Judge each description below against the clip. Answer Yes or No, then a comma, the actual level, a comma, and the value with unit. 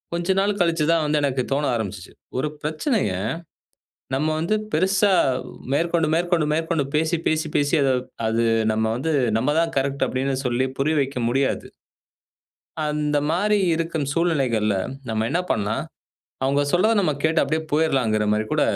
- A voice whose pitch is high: No, medium, 150 Hz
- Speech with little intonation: No, average, 3.9 semitones